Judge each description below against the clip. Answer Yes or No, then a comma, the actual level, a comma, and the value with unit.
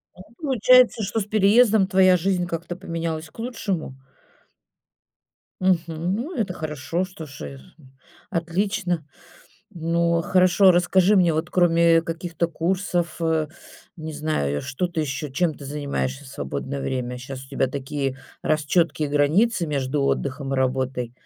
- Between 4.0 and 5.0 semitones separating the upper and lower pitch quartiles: Yes, average, 4.5 semitones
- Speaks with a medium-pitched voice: Yes, medium, 165 Hz